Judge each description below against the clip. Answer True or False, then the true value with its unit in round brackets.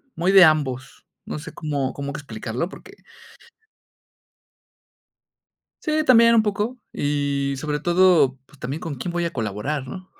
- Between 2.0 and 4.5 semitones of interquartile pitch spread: False (5.3 semitones)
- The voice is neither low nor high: True (150 Hz)